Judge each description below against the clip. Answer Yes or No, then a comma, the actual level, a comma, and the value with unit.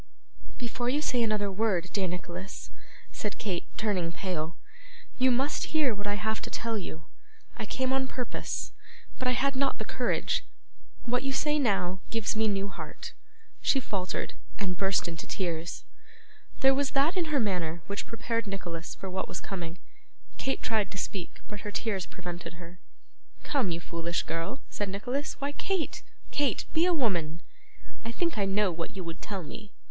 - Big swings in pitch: Yes, wide, 5.9 semitones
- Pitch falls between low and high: No, high, 205 Hz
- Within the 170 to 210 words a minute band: Yes, average, 175 wpm